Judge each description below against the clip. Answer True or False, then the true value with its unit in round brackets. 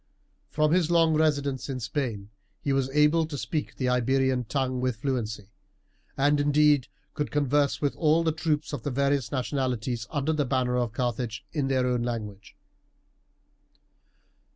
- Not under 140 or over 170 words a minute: True (155 wpm)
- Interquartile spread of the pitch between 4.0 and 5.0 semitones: False (3.0 semitones)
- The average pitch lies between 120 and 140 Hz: True (135 Hz)